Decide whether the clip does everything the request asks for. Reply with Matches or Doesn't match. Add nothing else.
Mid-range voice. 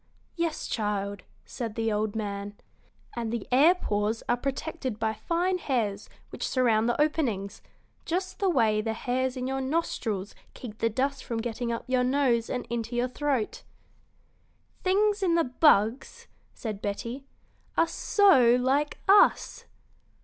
Doesn't match